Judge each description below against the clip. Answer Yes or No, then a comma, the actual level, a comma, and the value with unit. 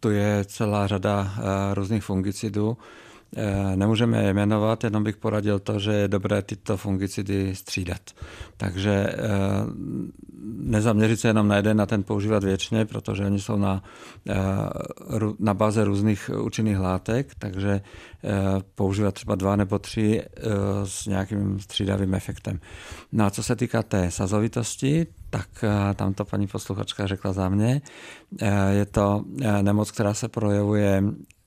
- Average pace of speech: Yes, average, 135 wpm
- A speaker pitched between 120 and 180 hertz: No, low, 100 Hz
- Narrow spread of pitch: Yes, narrow, 1.6 semitones